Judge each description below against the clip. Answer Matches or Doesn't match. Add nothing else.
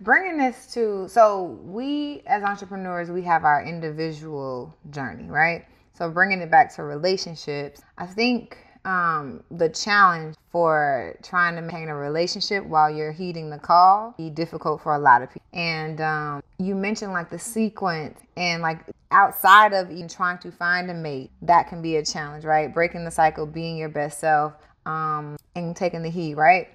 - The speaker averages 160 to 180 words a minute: Matches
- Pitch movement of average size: Matches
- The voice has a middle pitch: Matches